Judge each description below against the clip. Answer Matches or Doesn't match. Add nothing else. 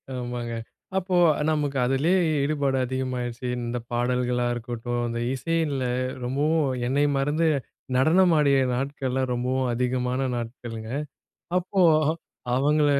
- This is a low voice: Matches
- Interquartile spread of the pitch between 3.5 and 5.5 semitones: Doesn't match